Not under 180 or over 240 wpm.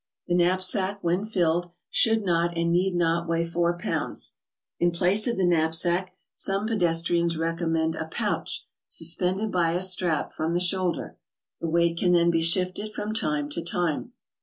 Yes: average, 185 wpm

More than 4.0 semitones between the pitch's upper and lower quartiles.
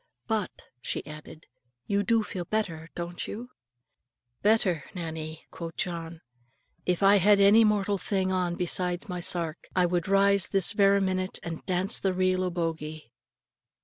No: average, 2.9 semitones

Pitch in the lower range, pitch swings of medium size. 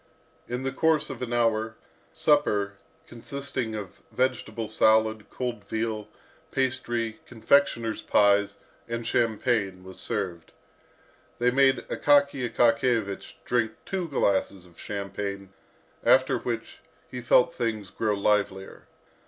Yes: low, 115 Hz; average, 3.7 semitones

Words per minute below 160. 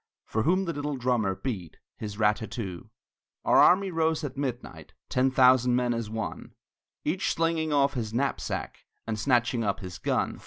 No: average, 170 wpm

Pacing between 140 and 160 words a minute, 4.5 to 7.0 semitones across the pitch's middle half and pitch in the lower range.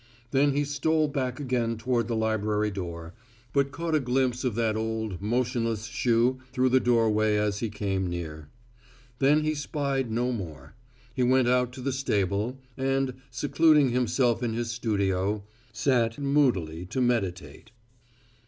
No: average, 150 wpm; average, 3.8 semitones; low, 120 Hz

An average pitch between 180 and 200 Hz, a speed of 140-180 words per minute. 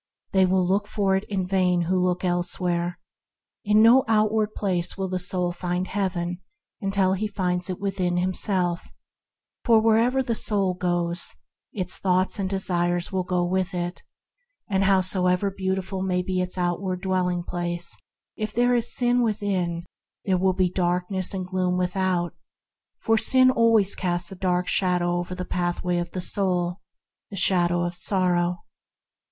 Yes: medium, 185 Hz; average, 155 wpm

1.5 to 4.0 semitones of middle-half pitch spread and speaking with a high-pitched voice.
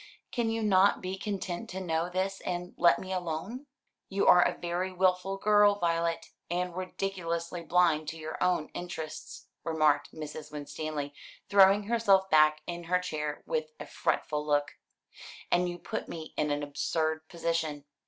No: average, 3.3 semitones; medium, 175 Hz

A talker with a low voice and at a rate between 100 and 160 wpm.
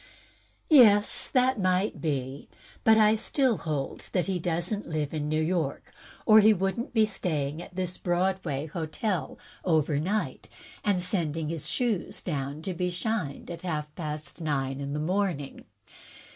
No: medium, 175 Hz; average, 155 wpm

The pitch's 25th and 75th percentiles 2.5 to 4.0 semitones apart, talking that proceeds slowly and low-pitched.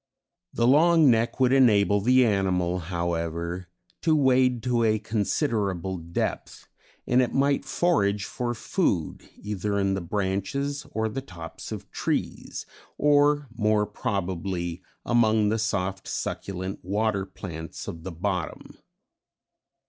No: average, 4.9 semitones; slow, 125 wpm; low, 105 Hz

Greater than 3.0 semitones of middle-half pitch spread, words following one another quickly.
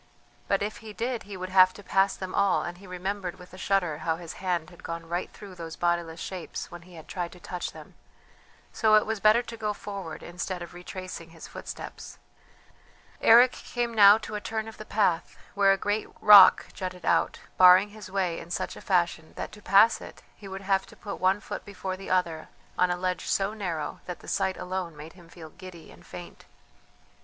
No: average, 2.7 semitones; fast, 215 wpm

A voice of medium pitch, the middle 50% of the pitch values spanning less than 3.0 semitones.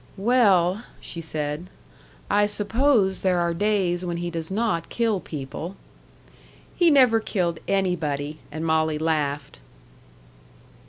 No: medium, 175 Hz; average, 4.5 semitones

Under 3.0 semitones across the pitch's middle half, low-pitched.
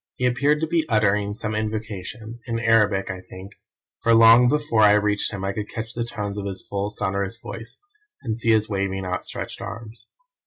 Yes: narrow, 2.5 semitones; low, 110 Hz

